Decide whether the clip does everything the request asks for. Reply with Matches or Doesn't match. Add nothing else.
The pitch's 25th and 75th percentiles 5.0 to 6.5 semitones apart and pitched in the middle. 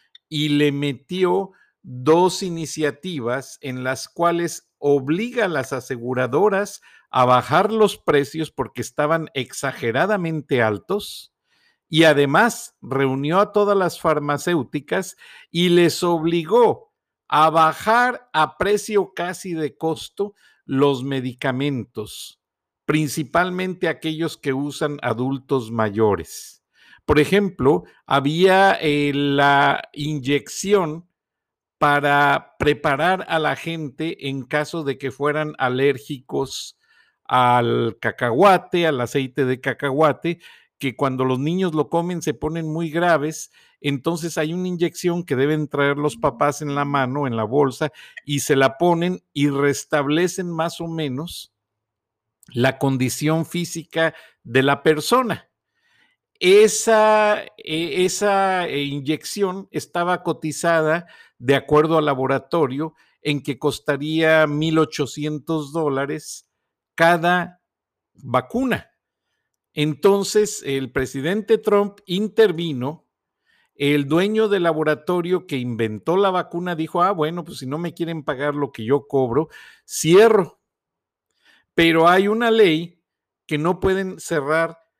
Doesn't match